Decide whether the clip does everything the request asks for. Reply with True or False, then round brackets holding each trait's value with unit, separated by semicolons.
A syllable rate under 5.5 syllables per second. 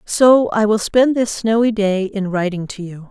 True (4.4 syllables/s)